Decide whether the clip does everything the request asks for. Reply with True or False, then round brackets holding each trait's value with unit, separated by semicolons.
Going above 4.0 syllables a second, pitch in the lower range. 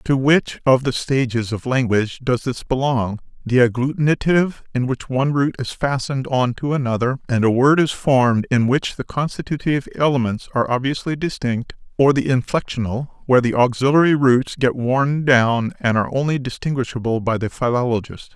True (5.4 syllables/s; 130 Hz)